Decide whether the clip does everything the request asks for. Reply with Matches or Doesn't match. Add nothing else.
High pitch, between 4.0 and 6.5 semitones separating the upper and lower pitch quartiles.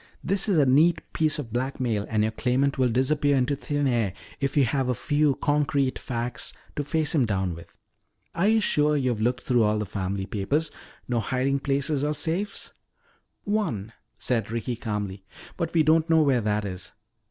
Doesn't match